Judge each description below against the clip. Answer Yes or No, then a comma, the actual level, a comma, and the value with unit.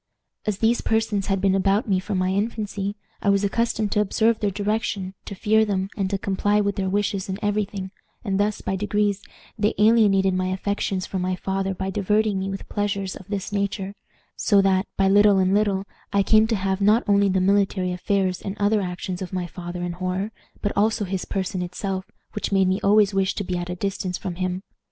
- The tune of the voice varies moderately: No, narrow, 1.6 semitones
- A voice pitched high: Yes, high, 195 Hz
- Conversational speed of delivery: No, fast, 210 wpm